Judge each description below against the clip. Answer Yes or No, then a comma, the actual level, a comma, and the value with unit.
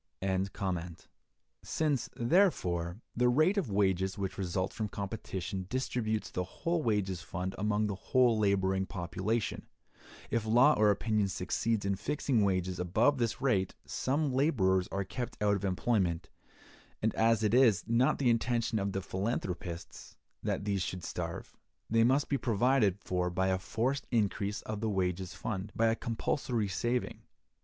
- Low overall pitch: Yes, low, 105 Hz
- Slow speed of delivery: No, average, 150 wpm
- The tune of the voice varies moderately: Yes, average, 4.1 semitones